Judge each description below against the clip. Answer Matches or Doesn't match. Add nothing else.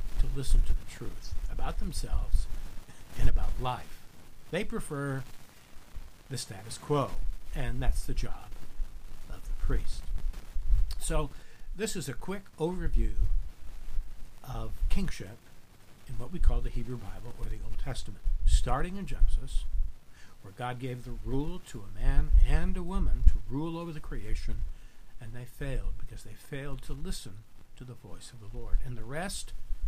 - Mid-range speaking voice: Doesn't match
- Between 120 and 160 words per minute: Matches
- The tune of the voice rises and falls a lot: Matches